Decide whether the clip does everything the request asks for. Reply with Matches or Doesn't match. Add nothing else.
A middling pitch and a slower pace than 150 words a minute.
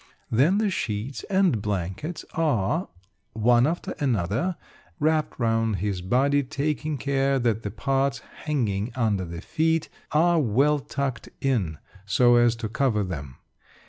Doesn't match